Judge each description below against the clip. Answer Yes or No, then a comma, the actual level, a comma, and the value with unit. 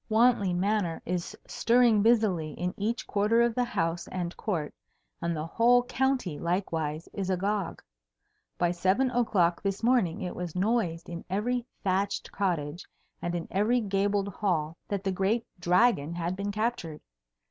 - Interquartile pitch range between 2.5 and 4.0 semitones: No, average, 4.5 semitones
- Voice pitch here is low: No, high, 195 Hz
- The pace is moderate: Yes, average, 150 wpm